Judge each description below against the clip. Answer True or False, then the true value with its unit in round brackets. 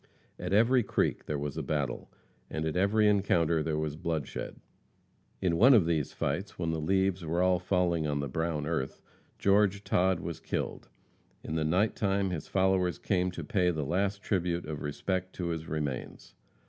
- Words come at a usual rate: True (180 wpm)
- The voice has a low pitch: True (85 Hz)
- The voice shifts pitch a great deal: False (3.7 semitones)